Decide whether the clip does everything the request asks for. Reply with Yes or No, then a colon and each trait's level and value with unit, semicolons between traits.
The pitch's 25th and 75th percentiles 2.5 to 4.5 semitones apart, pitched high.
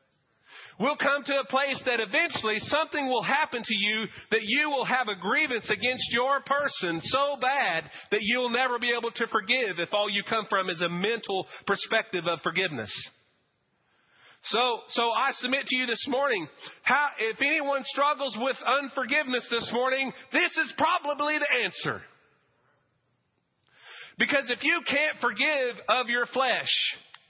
Yes: average, 3.9 semitones; very high, 250 Hz